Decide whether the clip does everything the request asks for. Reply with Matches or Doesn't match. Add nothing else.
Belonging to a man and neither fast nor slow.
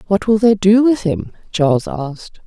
Doesn't match